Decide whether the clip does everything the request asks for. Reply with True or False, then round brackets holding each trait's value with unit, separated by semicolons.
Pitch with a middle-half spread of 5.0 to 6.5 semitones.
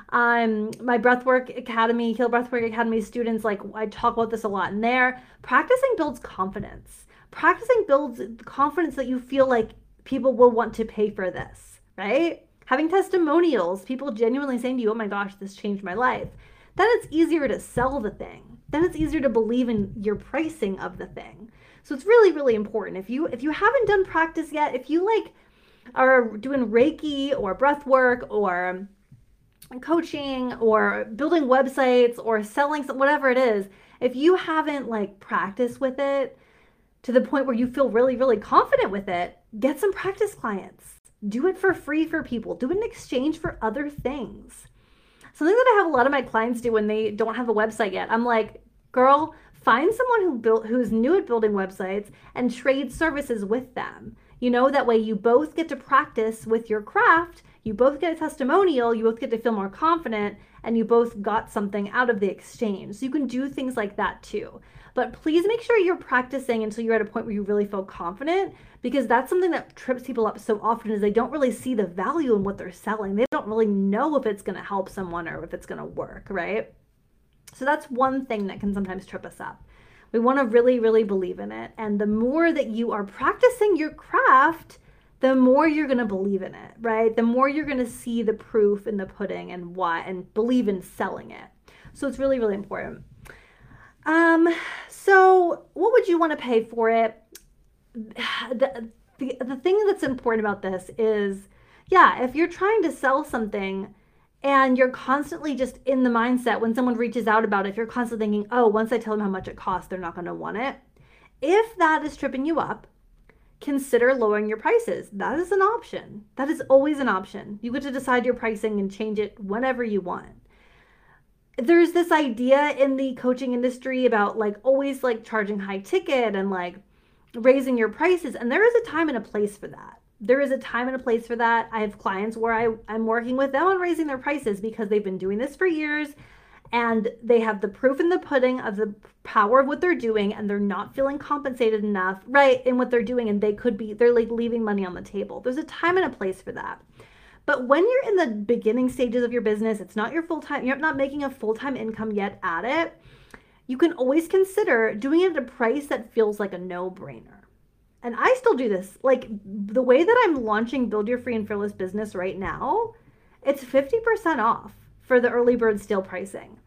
False (4.6 semitones)